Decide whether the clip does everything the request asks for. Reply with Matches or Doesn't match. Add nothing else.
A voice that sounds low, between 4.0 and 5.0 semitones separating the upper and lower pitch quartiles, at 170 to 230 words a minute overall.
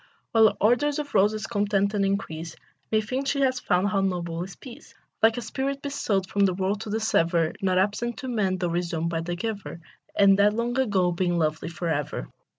Doesn't match